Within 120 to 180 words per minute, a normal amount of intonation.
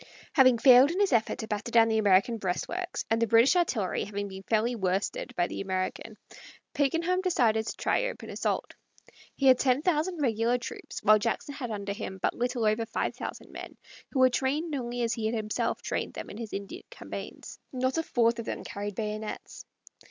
No: average, 195 wpm; average, 3.9 semitones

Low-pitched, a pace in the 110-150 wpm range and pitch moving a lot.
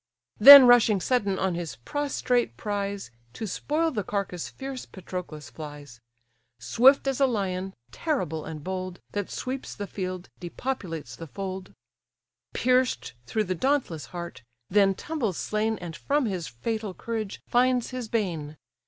No: high, 200 Hz; average, 140 wpm; wide, 6.0 semitones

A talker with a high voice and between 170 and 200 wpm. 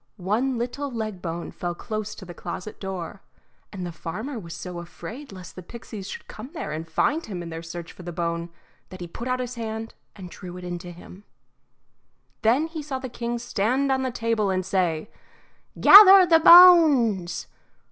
Yes: high, 210 Hz; average, 190 wpm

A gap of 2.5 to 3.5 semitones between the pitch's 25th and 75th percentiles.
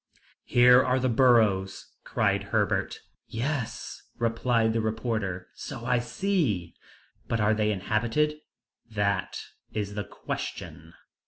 Yes: average, 3.2 semitones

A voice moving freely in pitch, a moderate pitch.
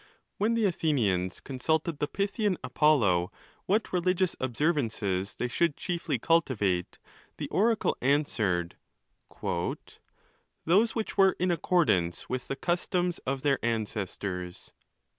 Yes: wide, 8.9 semitones; medium, 145 Hz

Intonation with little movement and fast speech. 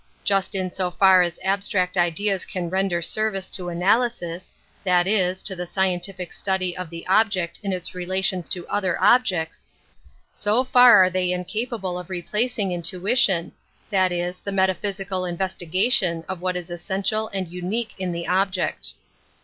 No: narrow, 1.9 semitones; average, 155 wpm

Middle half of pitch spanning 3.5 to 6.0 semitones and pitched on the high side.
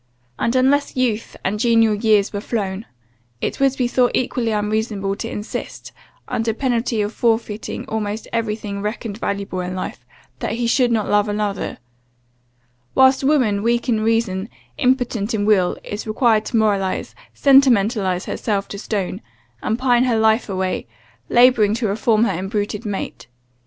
No: average, 2.7 semitones; high, 220 Hz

